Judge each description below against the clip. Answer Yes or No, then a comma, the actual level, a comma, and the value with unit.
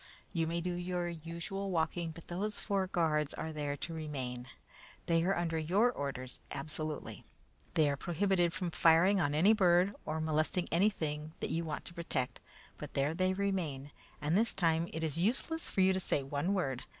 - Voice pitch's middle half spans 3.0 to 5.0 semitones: Yes, average, 3.4 semitones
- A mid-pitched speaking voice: Yes, medium, 165 Hz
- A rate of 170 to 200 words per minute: Yes, average, 185 wpm